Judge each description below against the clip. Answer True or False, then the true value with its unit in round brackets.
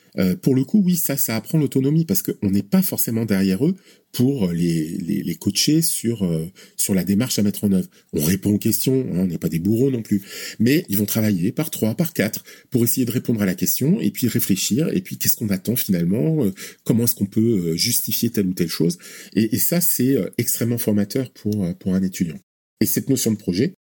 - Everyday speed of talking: False (230 wpm)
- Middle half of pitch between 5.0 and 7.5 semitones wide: True (5.4 semitones)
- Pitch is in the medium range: False (110 Hz)